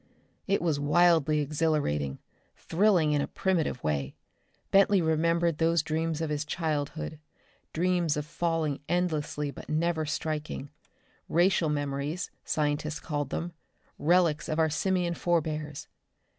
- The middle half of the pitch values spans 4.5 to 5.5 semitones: No, narrow, 2.4 semitones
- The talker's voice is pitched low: No, medium, 155 Hz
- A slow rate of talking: Yes, slow, 120 wpm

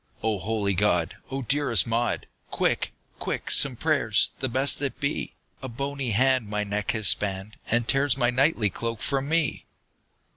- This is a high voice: No, low, 120 Hz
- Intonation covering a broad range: No, average, 4.6 semitones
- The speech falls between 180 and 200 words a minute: No, average, 160 wpm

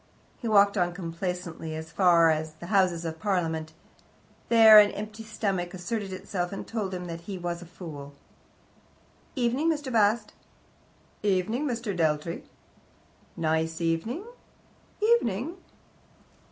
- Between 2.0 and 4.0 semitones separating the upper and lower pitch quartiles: No, average, 4.6 semitones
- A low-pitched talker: No, medium, 185 Hz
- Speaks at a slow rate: Yes, slow, 120 wpm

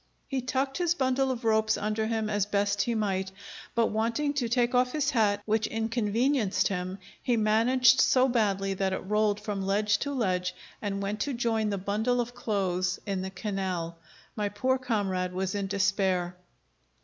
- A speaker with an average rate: Yes, average, 175 wpm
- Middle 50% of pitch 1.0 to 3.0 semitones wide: No, average, 3.7 semitones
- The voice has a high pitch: Yes, high, 215 Hz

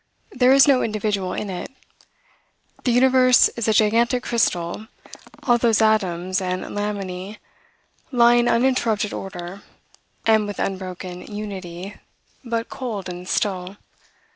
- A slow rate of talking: Yes, slow, 120 wpm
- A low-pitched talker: No, high, 210 Hz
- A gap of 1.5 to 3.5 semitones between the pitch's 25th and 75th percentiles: No, average, 4.1 semitones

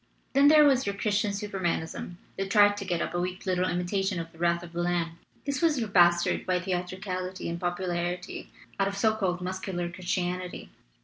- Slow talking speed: No, average, 195 wpm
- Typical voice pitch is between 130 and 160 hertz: No, medium, 185 Hz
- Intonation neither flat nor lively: No, narrow, 2.3 semitones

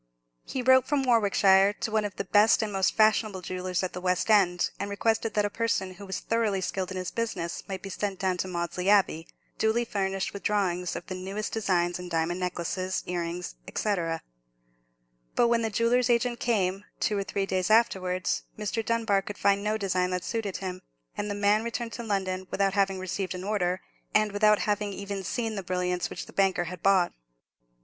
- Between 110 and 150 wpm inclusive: No, average, 200 wpm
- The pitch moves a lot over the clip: No, average, 2.7 semitones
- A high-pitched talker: Yes, high, 195 Hz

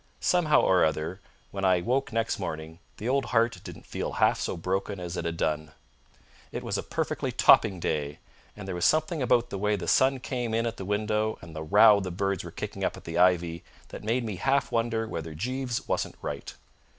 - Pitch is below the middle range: Yes, low, 100 Hz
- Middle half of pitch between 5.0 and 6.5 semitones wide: Yes, average, 5.3 semitones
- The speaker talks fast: Yes, fast, 210 wpm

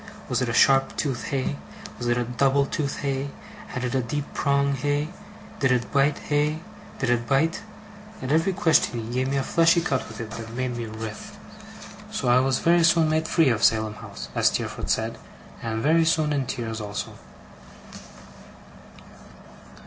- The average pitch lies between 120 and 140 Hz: Yes, low, 135 Hz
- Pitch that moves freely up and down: No, average, 3.7 semitones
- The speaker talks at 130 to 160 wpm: No, average, 180 wpm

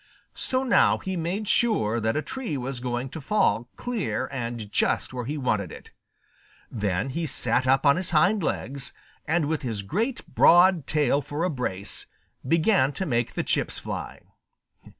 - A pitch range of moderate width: No, wide, 6.5 semitones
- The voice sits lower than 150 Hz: Yes, medium, 140 Hz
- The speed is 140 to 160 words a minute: No, average, 170 wpm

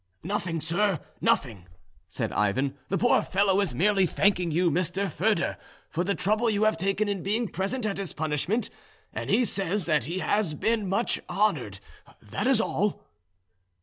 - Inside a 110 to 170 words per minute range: Yes, average, 165 wpm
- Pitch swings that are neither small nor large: Yes, average, 4.1 semitones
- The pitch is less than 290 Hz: Yes, high, 190 Hz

